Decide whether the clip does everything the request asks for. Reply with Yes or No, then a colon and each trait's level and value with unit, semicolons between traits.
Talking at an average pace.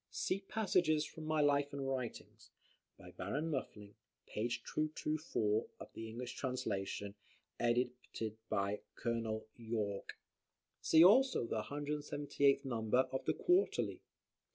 No: slow, 115 wpm